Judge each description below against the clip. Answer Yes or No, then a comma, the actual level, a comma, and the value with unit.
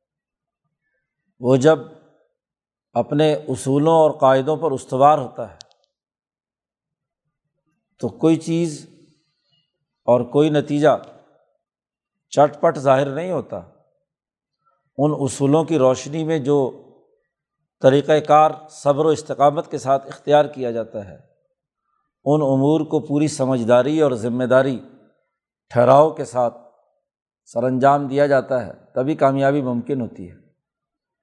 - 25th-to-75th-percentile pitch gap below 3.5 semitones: Yes, average, 2.7 semitones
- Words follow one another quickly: No, average, 115 wpm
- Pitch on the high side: No, medium, 150 Hz